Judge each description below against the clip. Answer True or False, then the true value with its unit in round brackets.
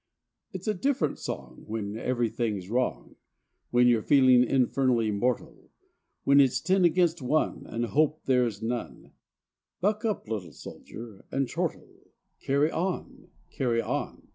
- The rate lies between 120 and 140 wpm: True (135 wpm)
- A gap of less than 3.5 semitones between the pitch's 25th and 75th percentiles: False (5.2 semitones)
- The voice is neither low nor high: False (125 Hz)